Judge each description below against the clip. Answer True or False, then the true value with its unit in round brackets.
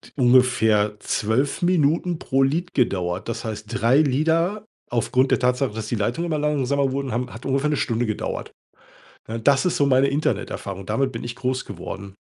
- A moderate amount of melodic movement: True (4.1 semitones)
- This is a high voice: False (130 Hz)